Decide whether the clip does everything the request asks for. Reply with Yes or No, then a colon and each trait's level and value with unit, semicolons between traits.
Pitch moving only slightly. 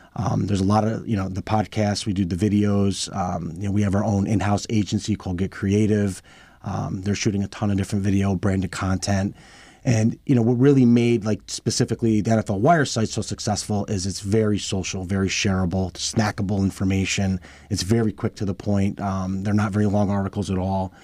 Yes: narrow, 2.0 semitones